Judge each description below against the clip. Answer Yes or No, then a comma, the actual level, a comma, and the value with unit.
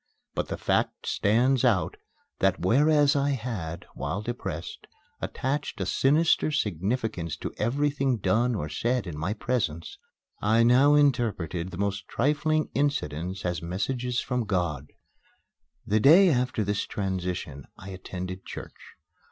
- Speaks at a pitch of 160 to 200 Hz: No, low, 110 Hz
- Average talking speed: No, slow, 130 wpm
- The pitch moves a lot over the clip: Yes, wide, 6.4 semitones